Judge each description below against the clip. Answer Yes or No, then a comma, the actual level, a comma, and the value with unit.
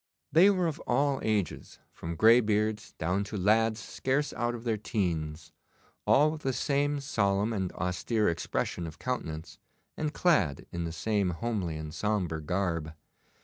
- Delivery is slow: No, average, 150 wpm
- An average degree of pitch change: No, wide, 6.5 semitones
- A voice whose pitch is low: Yes, low, 105 Hz